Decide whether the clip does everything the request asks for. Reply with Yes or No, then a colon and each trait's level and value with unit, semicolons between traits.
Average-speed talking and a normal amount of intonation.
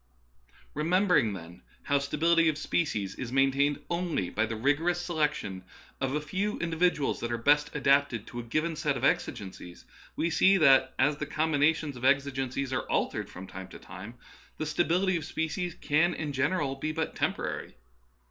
Yes: average, 180 wpm; average, 4.0 semitones